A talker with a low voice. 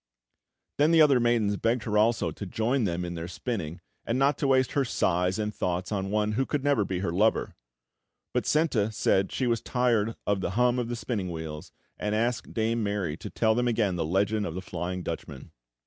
Yes: low, 105 Hz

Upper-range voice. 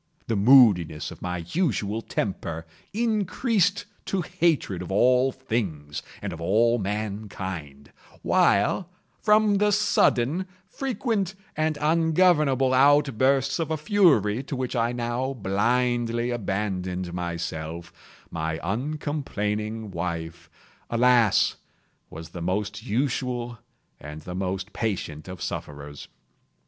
No: low, 115 Hz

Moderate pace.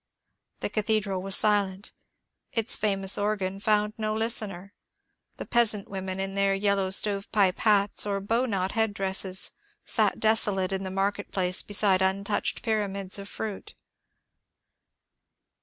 No: slow, 130 wpm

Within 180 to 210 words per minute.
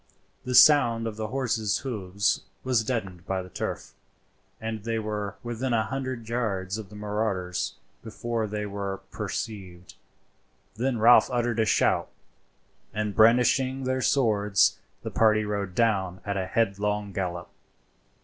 No: average, 140 wpm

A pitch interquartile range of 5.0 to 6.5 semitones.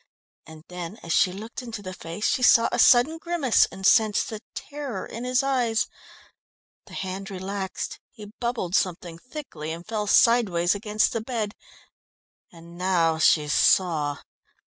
Yes: average, 5.3 semitones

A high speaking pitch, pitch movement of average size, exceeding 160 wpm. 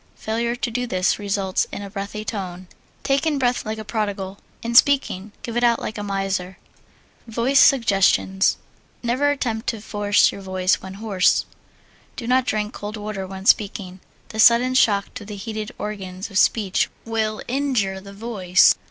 Yes: high, 210 Hz; average, 3.2 semitones; average, 170 wpm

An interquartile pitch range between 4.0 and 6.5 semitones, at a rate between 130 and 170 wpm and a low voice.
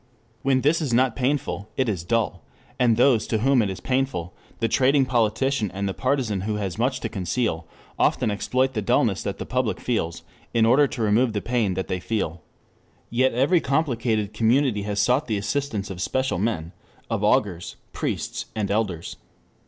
No: average, 4.5 semitones; average, 180 wpm; low, 115 Hz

